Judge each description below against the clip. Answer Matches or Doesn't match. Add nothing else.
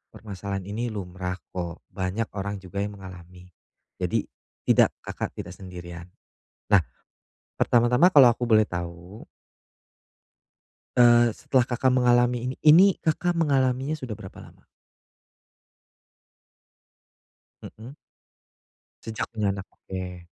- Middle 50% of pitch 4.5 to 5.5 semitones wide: Matches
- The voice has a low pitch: Matches